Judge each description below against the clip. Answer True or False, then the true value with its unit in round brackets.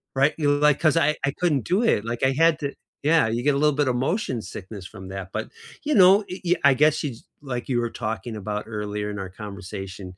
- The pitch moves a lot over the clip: True (6.4 semitones)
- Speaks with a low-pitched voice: True (130 Hz)